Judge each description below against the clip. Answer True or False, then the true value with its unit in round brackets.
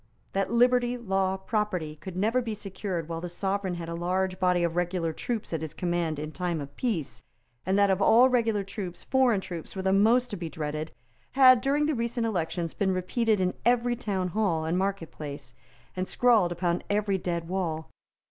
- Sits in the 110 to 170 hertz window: False (190 Hz)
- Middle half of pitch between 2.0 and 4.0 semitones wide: False (4.4 semitones)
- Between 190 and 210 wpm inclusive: True (195 wpm)